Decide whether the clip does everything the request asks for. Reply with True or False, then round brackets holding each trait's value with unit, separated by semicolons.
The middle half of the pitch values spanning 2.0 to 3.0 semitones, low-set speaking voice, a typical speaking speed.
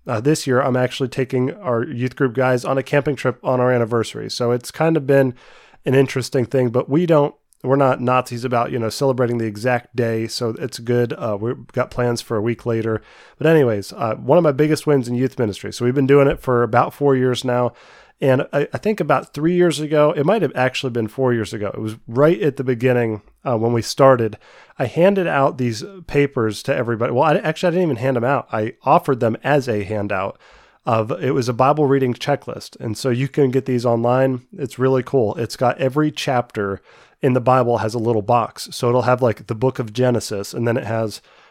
False (2.7 semitones; 125 Hz; 225 wpm)